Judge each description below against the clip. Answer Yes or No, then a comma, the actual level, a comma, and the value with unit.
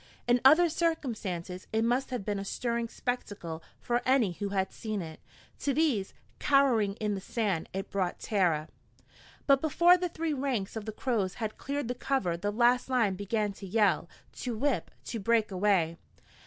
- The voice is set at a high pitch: Yes, high, 220 Hz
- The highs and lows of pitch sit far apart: No, average, 4.8 semitones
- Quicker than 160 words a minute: Yes, average, 175 wpm